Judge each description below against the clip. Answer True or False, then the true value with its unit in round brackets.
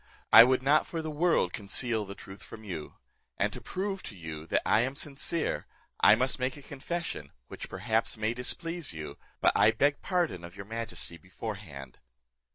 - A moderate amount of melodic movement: False (7.0 semitones)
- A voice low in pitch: True (115 Hz)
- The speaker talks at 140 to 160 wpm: False (180 wpm)